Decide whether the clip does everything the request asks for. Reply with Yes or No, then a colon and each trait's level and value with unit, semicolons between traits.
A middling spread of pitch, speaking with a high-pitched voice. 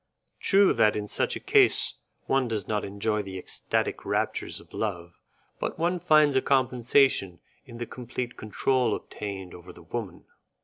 No: average, 4.8 semitones; low, 115 Hz